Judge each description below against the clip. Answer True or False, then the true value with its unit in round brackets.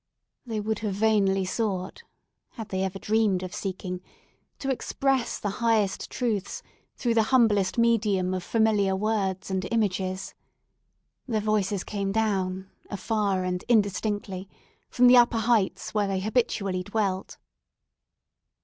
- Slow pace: True (120 wpm)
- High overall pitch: True (205 Hz)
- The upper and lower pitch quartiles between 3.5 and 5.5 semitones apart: False (2.8 semitones)